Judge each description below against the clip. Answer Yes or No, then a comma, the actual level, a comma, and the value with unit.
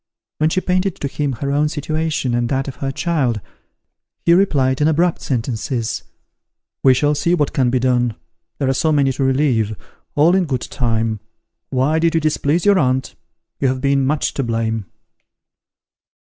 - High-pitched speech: No, medium, 140 Hz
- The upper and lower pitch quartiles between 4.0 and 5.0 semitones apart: No, average, 3.6 semitones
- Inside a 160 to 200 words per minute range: Yes, average, 175 wpm